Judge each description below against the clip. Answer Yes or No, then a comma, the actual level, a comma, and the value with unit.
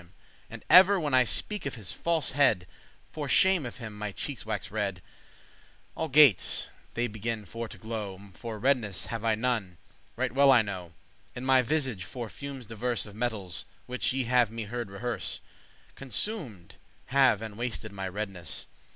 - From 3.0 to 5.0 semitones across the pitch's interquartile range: Yes, average, 4.2 semitones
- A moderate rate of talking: Yes, average, 170 wpm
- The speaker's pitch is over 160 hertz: No, low, 115 Hz